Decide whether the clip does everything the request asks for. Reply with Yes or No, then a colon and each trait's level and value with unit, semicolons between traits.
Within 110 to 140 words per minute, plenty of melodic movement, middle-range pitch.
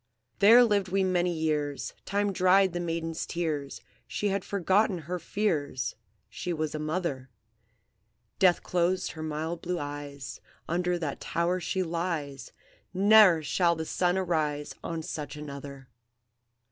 No: slow, 135 wpm; average, 3.6 semitones; medium, 170 Hz